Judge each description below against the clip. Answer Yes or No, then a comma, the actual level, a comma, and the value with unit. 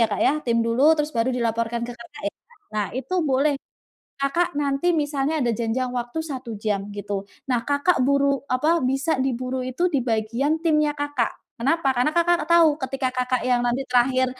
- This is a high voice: Yes, very high, 260 Hz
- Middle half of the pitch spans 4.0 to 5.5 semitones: No, average, 3.4 semitones